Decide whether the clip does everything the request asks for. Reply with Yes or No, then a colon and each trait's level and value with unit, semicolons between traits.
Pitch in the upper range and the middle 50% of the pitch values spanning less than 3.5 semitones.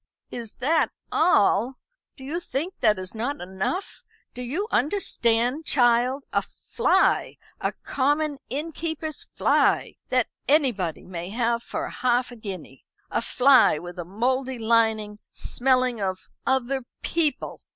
No: very high, 250 Hz; average, 4.5 semitones